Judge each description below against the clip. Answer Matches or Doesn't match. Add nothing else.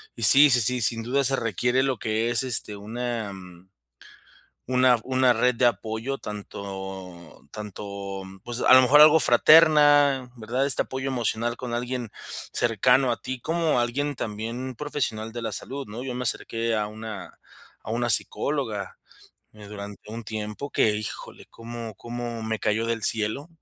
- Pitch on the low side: Matches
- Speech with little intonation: Doesn't match